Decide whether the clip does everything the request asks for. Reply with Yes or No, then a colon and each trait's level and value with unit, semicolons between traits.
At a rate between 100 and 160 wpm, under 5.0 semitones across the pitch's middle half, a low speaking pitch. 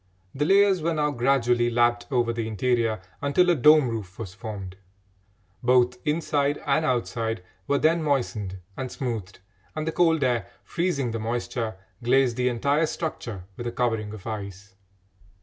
Yes: average, 155 wpm; average, 4.4 semitones; low, 120 Hz